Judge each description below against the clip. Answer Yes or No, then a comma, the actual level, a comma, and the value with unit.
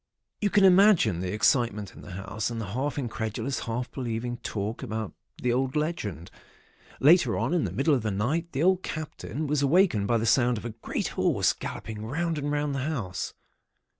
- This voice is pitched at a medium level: No, low, 125 Hz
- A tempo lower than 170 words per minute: No, average, 195 wpm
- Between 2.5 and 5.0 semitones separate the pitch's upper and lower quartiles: No, wide, 5.5 semitones